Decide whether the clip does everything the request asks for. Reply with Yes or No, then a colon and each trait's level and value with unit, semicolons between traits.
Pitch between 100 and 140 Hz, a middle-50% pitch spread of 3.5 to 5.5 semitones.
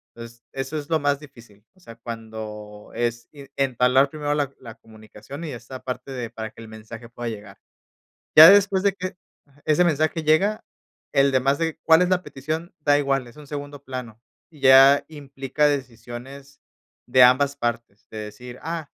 Yes: low, 135 Hz; average, 4.0 semitones